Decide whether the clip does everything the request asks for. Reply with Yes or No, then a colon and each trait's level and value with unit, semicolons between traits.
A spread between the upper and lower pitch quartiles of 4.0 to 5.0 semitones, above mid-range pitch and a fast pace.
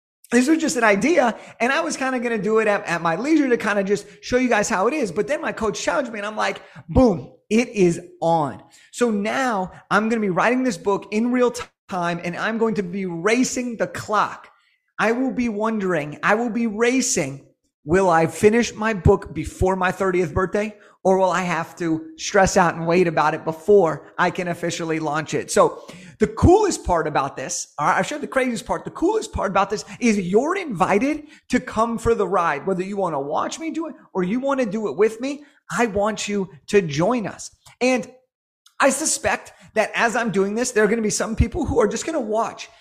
Yes: average, 4.7 semitones; high, 210 Hz; fast, 225 wpm